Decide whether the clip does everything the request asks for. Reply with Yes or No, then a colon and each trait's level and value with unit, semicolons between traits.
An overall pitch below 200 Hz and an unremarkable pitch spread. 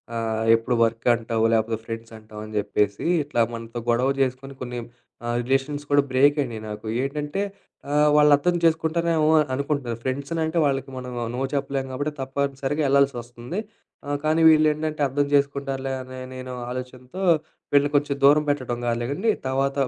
Yes: low, 135 Hz; average, 3.3 semitones